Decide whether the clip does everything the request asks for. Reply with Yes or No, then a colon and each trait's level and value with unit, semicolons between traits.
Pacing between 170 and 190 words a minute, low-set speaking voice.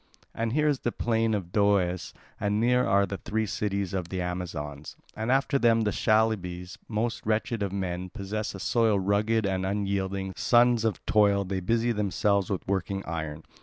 Yes: average, 175 wpm; low, 100 Hz